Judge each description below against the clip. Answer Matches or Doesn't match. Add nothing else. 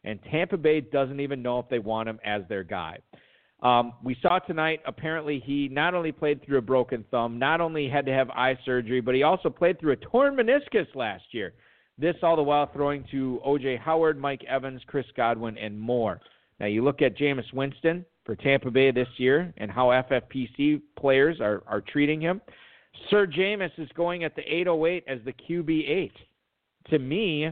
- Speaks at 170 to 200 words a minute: Matches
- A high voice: Doesn't match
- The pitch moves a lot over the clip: Doesn't match